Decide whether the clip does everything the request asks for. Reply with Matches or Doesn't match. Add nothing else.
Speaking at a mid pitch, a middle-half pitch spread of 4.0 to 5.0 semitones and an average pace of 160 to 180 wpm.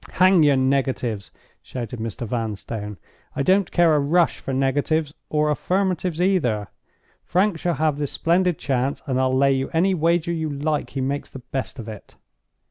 Matches